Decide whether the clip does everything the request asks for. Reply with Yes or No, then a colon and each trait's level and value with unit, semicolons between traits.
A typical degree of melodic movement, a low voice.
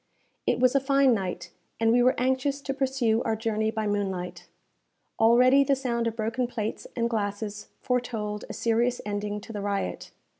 No: average, 3.3 semitones; high, 230 Hz